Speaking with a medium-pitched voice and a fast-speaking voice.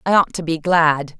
Yes: medium, 165 Hz; fast, 250 wpm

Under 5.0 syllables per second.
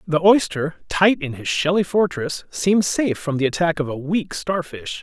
Yes: 4.7 syllables/s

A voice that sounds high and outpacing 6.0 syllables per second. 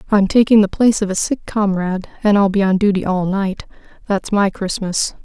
No: high, 200 Hz; 5.5 syllables/s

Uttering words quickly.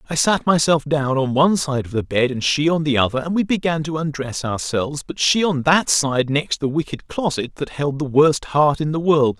Yes: fast, 245 wpm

